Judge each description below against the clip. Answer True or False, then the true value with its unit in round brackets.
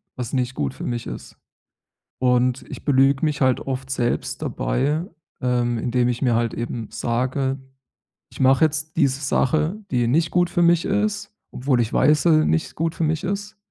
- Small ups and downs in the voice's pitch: False (4.3 semitones)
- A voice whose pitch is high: False (135 Hz)